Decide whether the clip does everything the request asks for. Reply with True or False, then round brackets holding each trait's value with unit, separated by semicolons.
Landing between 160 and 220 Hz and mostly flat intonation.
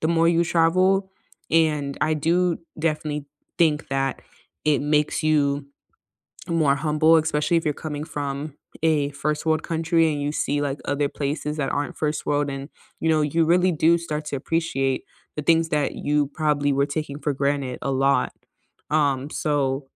False (150 Hz; 2.2 semitones)